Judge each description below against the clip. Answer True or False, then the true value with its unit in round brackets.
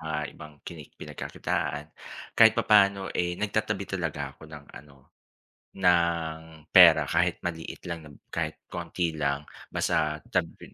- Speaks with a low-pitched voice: True (80 Hz)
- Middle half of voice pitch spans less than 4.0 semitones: True (2.7 semitones)